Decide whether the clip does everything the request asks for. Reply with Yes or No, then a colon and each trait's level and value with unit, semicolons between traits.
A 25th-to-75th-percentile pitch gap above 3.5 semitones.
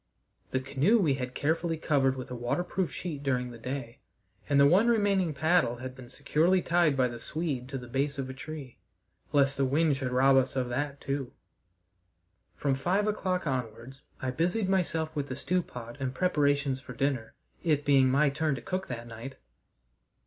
Yes: average, 3.9 semitones